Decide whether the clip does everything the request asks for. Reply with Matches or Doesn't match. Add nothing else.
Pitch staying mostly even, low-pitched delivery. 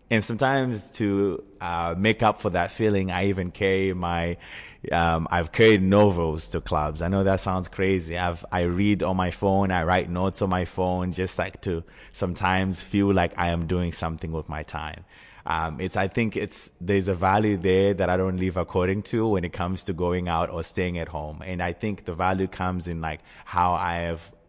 Matches